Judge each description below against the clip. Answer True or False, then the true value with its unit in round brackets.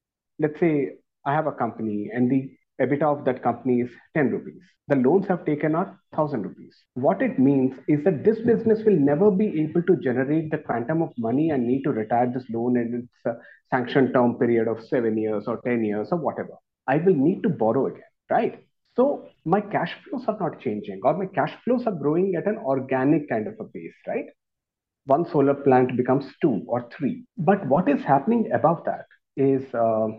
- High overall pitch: False (140 Hz)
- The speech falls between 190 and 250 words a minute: True (200 wpm)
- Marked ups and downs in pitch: True (6.0 semitones)